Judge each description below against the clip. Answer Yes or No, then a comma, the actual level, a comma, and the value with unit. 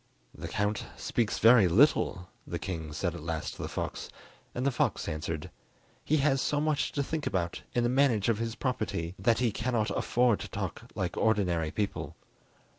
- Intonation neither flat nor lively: No, wide, 6.1 semitones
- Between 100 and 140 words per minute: No, average, 185 wpm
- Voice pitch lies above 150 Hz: No, low, 110 Hz